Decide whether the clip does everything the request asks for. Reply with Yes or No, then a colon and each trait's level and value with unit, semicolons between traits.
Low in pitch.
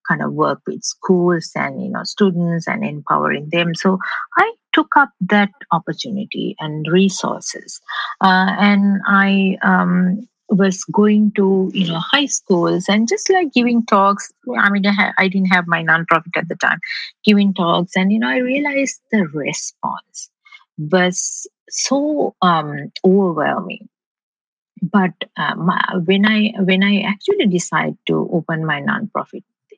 No: high, 195 Hz